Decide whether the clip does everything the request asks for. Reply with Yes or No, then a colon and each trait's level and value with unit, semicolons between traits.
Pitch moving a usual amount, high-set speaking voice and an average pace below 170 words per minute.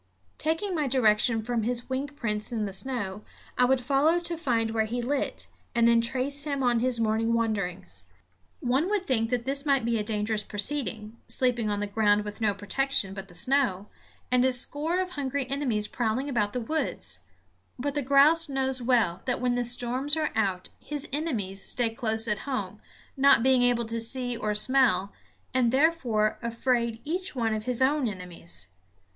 No: average, 4.0 semitones; high, 245 Hz; average, 185 wpm